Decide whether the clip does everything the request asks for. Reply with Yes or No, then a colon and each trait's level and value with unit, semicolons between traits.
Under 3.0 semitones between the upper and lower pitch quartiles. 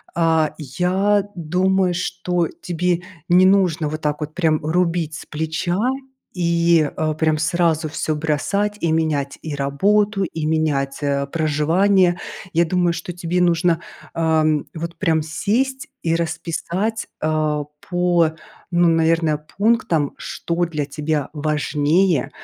Yes: narrow, 2.5 semitones